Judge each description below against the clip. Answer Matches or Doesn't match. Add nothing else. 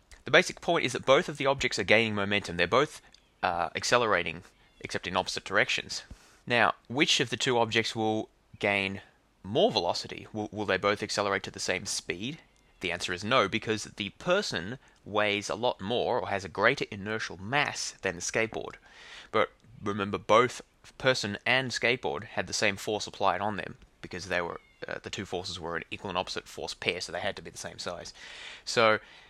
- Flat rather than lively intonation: Matches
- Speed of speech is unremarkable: Matches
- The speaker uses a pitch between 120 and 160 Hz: Doesn't match